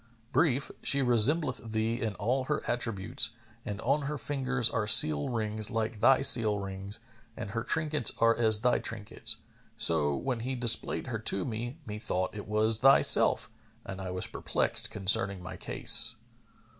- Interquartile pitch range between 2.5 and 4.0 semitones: Yes, average, 3.5 semitones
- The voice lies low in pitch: Yes, low, 115 Hz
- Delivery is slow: No, average, 155 wpm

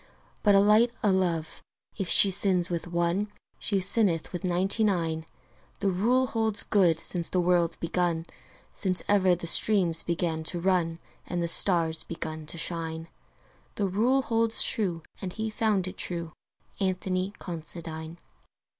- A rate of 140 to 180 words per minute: Yes, average, 150 wpm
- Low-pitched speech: No, medium, 180 Hz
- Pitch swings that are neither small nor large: Yes, average, 3.1 semitones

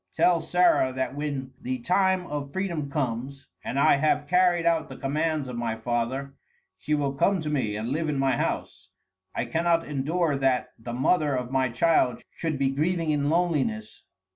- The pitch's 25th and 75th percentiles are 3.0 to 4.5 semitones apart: Yes, average, 4.1 semitones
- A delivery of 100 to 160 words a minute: No, average, 180 wpm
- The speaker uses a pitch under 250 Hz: Yes, medium, 140 Hz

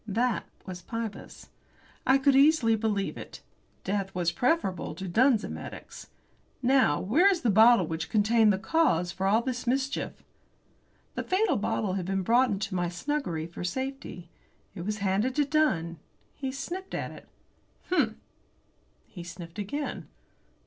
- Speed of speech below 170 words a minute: Yes, average, 150 wpm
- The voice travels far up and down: Yes, wide, 6.3 semitones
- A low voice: No, high, 220 Hz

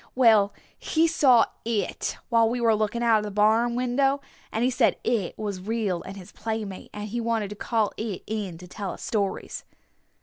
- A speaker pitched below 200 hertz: No, high, 220 Hz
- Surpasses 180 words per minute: Yes, average, 195 wpm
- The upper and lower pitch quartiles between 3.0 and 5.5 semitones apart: No, narrow, 2.5 semitones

